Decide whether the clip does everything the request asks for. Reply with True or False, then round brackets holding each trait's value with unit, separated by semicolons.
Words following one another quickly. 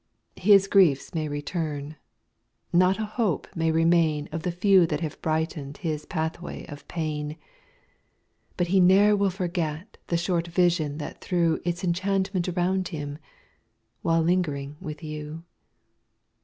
False (140 wpm)